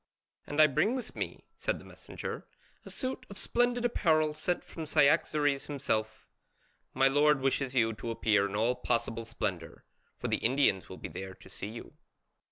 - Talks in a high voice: No, low, 135 Hz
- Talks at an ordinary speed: Yes, average, 175 wpm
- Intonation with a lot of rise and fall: Yes, wide, 5.8 semitones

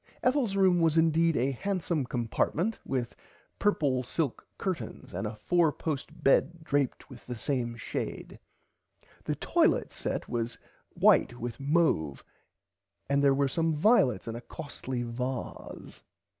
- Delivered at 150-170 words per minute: No, slow, 135 wpm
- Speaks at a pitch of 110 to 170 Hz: Yes, medium, 140 Hz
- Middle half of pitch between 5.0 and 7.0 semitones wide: Yes, average, 5.3 semitones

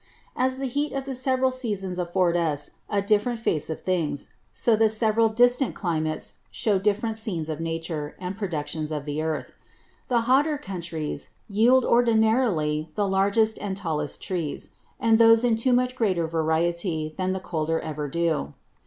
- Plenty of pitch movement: Yes, wide, 6.1 semitones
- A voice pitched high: Yes, high, 195 Hz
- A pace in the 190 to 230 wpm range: No, average, 160 wpm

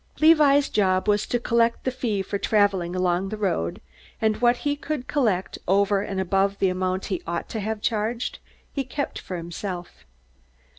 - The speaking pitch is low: No, high, 205 Hz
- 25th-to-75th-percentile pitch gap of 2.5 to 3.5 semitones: No, average, 4.2 semitones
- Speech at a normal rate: Yes, average, 170 wpm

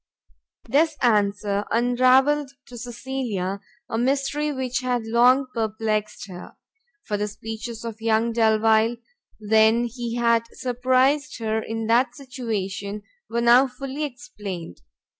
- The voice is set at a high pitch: Yes, high, 235 Hz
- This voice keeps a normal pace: No, slow, 120 wpm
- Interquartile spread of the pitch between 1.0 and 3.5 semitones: Yes, average, 2.8 semitones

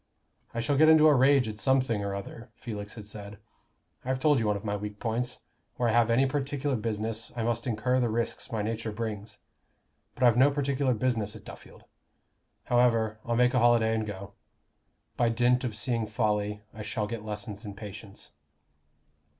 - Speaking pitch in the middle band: No, low, 115 Hz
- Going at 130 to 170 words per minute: No, average, 185 wpm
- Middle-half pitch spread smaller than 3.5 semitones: Yes, average, 2.9 semitones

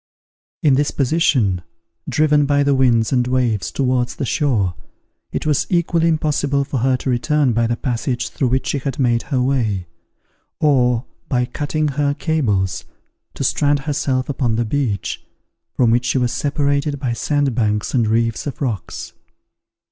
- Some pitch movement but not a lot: Yes, average, 3.3 semitones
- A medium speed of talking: Yes, average, 155 wpm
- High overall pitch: No, low, 130 Hz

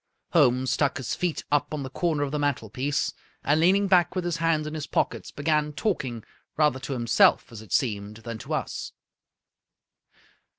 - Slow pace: No, average, 175 wpm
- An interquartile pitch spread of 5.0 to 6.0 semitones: No, average, 4.0 semitones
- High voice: No, medium, 145 Hz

